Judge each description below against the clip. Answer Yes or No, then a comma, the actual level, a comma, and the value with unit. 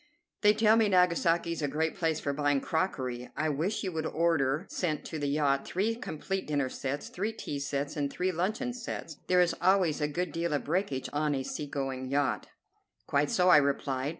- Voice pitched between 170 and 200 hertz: No, medium, 155 Hz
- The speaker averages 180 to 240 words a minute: Yes, fast, 205 wpm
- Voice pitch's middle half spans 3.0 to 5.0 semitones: Yes, average, 4.2 semitones